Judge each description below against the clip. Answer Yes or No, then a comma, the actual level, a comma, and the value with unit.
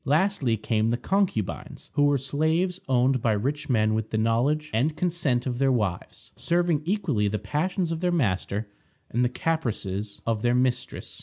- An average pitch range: No, wide, 6.2 semitones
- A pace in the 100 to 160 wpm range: No, average, 170 wpm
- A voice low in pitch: Yes, low, 130 Hz